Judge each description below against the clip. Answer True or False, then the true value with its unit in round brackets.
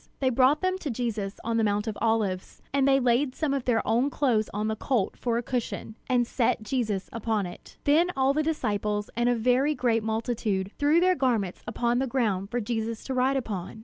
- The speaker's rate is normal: False (210 wpm)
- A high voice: True (235 Hz)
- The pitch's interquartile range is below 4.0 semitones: True (3.6 semitones)